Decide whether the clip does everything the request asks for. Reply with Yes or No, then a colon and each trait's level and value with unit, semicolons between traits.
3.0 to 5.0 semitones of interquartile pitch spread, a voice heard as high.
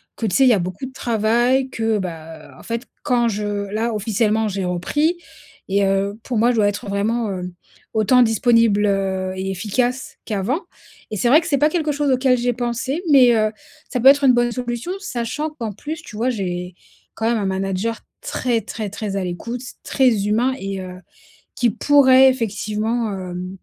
Yes: average, 4.2 semitones; high, 225 Hz